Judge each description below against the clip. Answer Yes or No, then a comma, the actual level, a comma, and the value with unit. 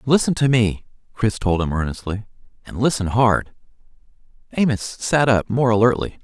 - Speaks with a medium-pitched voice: No, low, 110 Hz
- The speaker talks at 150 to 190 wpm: Yes, average, 155 wpm